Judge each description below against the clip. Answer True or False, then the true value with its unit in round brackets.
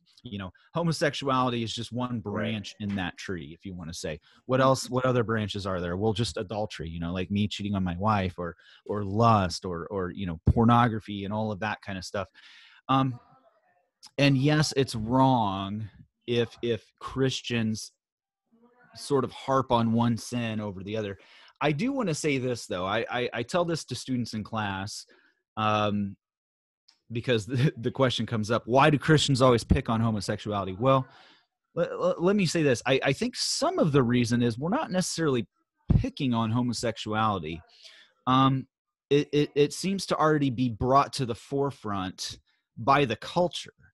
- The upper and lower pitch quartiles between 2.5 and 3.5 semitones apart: False (4.7 semitones)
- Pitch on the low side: True (120 Hz)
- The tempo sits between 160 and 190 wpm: True (175 wpm)